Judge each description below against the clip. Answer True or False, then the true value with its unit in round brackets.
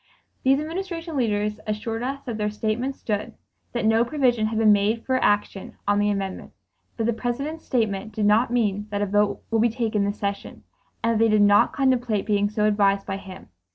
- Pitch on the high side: True (215 Hz)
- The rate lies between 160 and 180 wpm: False (200 wpm)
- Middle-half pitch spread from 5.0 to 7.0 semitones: False (2.9 semitones)